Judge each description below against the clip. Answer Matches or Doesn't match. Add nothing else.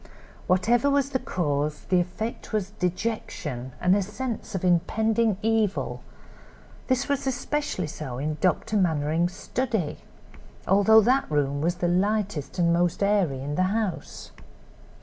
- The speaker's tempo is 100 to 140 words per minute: Matches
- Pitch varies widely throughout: Doesn't match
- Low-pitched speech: Doesn't match